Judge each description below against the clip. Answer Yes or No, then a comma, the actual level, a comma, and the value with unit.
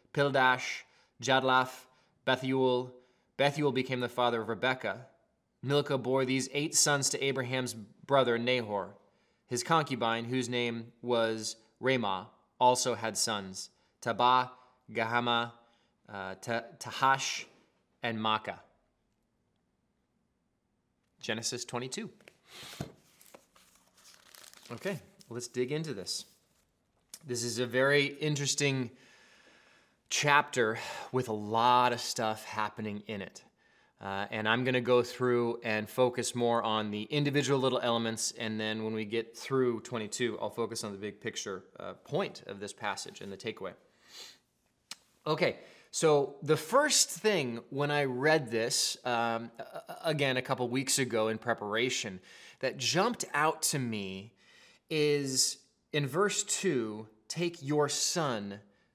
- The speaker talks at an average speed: No, slow, 120 wpm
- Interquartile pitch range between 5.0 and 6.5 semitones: No, average, 3.3 semitones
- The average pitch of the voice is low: Yes, low, 125 Hz